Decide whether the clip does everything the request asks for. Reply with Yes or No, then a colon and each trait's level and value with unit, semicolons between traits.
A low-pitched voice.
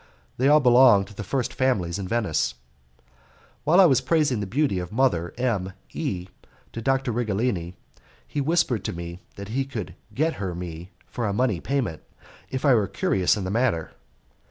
Yes: low, 115 Hz